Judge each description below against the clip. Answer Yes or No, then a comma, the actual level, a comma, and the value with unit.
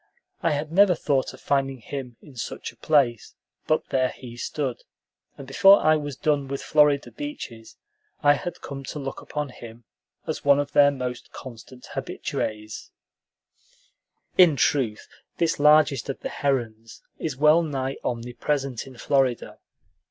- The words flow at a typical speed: Yes, average, 150 wpm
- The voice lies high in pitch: No, medium, 140 Hz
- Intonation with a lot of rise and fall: No, average, 3.0 semitones